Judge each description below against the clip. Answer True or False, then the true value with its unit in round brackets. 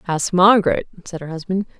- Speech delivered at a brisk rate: False (165 wpm)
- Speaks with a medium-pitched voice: True (180 Hz)